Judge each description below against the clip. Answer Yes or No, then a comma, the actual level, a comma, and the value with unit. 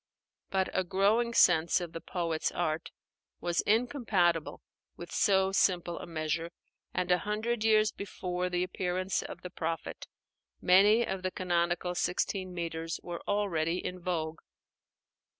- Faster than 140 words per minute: No, slow, 135 wpm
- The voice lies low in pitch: No, medium, 180 Hz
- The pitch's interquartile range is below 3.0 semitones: Yes, narrow, 2.4 semitones